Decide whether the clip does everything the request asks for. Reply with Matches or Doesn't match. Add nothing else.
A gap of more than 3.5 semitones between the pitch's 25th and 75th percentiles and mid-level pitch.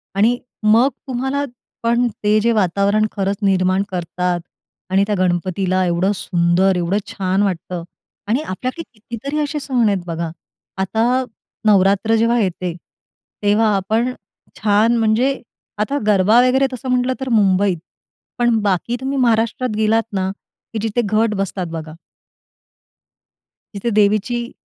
Doesn't match